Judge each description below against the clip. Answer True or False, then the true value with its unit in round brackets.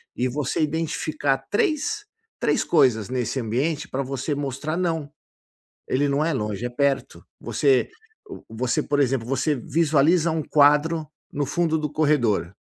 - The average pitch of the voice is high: False (145 Hz)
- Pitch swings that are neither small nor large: True (3.4 semitones)